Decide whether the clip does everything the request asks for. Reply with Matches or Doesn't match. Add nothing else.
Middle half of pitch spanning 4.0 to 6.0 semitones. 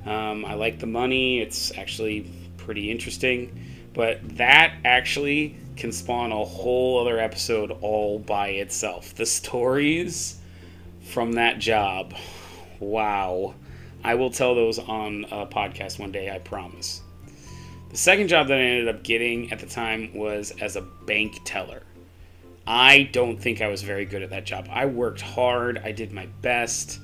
Matches